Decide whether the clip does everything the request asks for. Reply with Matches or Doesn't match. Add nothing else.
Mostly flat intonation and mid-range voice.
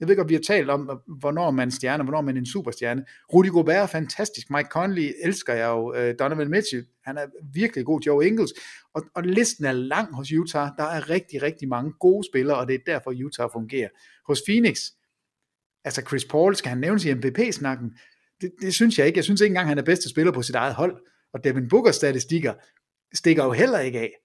Doesn't match